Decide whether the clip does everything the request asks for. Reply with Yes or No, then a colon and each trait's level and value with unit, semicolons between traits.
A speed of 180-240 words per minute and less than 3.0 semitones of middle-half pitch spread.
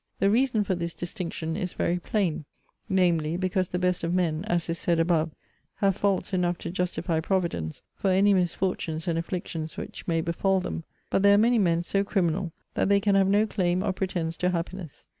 Yes: average, 195 wpm; narrow, 2.5 semitones